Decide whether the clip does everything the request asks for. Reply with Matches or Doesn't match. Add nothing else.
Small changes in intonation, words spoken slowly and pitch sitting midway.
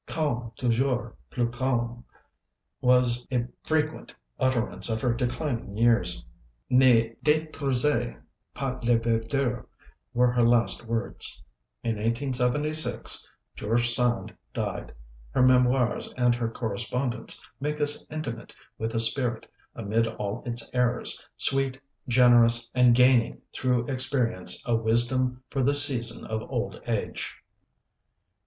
Doesn't match